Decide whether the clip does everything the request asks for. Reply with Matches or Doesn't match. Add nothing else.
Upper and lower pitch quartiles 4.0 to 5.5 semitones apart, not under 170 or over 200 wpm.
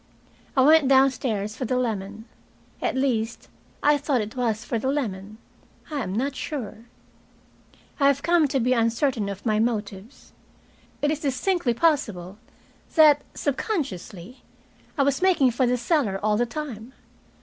Doesn't match